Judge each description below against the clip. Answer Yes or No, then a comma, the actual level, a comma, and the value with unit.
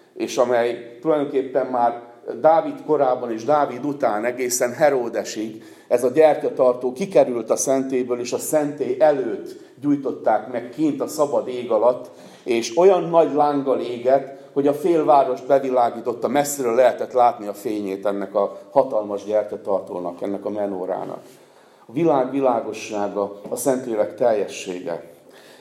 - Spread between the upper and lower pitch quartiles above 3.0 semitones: Yes, average, 4.4 semitones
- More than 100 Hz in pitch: Yes, low, 130 Hz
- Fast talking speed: No, average, 130 wpm